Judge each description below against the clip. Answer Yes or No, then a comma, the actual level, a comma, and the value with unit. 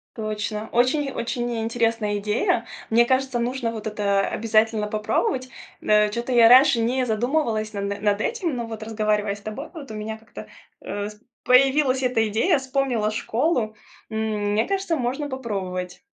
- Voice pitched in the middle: No, high, 225 Hz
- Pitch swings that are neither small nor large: Yes, average, 3.4 semitones